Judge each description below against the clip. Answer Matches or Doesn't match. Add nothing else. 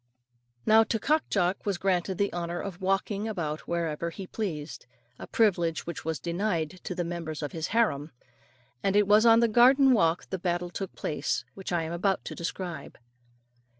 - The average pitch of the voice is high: Doesn't match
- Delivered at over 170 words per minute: Matches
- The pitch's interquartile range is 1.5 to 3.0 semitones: Doesn't match